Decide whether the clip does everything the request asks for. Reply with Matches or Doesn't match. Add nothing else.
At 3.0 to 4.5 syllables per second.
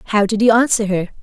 Doesn't match